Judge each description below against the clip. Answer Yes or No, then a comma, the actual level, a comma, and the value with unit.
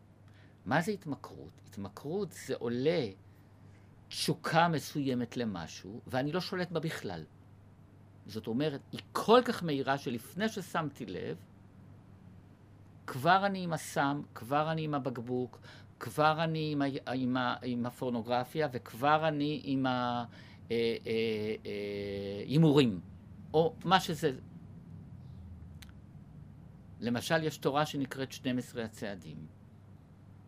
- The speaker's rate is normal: Yes, average, 110 wpm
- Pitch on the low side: Yes, low, 120 Hz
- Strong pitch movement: Yes, wide, 6.8 semitones